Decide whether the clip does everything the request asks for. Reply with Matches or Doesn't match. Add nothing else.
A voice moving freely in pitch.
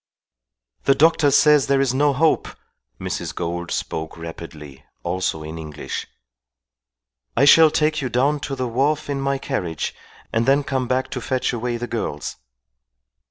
Matches